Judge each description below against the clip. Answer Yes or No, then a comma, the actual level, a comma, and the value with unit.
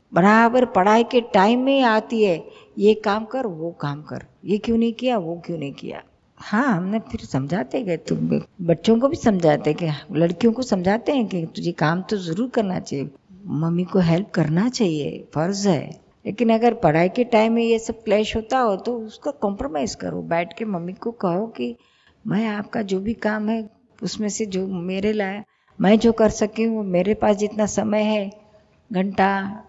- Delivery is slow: No, fast, 190 wpm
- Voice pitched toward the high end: Yes, high, 210 Hz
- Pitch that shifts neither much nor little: Yes, average, 4.0 semitones